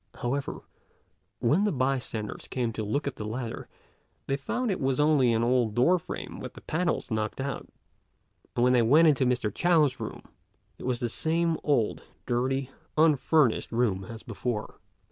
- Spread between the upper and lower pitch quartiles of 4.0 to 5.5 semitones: Yes, average, 4.3 semitones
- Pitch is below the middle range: Yes, low, 130 Hz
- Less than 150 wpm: No, average, 165 wpm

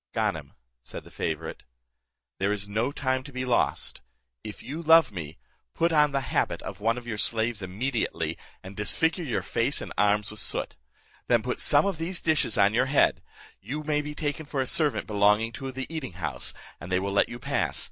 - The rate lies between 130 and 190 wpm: No, average, 200 wpm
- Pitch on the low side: Yes, low, 125 Hz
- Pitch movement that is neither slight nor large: No, wide, 6.1 semitones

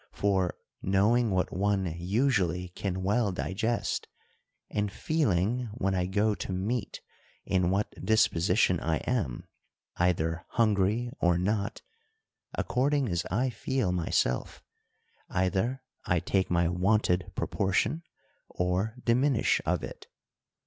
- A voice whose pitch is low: Yes, very low, 95 Hz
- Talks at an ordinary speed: No, slow, 115 wpm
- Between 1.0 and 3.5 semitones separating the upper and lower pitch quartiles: No, average, 4.0 semitones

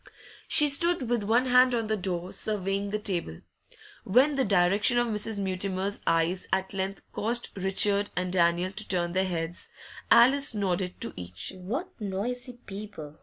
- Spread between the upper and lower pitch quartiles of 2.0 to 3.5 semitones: No, average, 4.2 semitones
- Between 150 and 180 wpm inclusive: Yes, average, 160 wpm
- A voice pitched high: Yes, high, 200 Hz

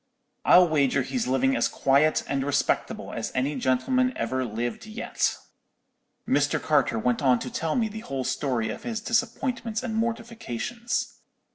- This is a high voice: No, medium, 145 Hz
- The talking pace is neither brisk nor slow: Yes, average, 150 wpm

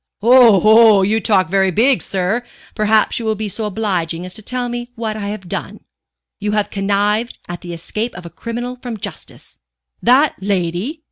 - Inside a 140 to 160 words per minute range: No, average, 185 wpm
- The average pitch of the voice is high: Yes, high, 210 Hz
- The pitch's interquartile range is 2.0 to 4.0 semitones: Yes, average, 3.4 semitones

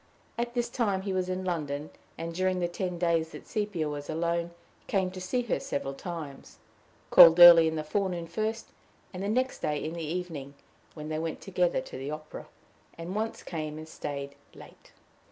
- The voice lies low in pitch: No, medium, 170 Hz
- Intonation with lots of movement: No, average, 3.3 semitones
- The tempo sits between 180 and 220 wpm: Yes, average, 185 wpm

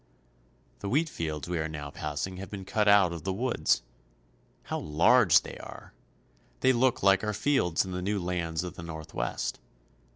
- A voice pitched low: Yes, very low, 90 Hz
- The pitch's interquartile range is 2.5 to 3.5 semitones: No, average, 4.4 semitones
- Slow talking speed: No, average, 175 wpm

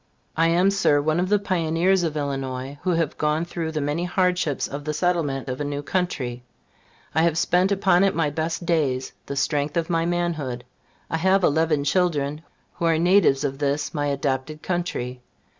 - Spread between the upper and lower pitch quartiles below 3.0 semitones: No, average, 3.5 semitones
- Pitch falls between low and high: Yes, medium, 160 Hz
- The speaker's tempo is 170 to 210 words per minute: Yes, average, 185 wpm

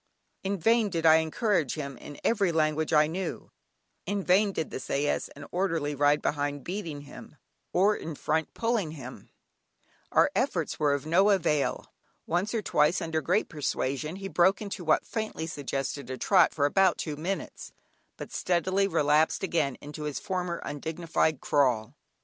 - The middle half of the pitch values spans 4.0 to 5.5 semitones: Yes, average, 4.5 semitones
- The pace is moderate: Yes, average, 160 wpm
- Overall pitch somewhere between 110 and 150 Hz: No, medium, 160 Hz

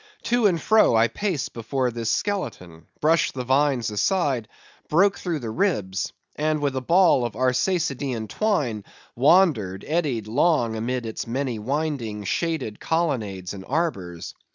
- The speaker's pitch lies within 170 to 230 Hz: No, low, 130 Hz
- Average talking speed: No, slow, 130 wpm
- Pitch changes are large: Yes, wide, 6.8 semitones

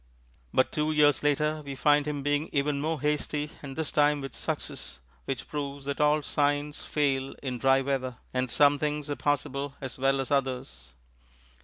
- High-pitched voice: No, medium, 145 Hz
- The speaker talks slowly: No, average, 175 wpm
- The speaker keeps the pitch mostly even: Yes, narrow, 1.7 semitones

